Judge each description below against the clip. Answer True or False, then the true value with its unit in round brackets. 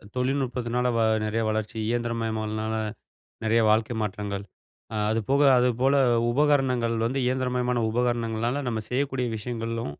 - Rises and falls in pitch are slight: True (2.2 semitones)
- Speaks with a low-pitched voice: True (120 Hz)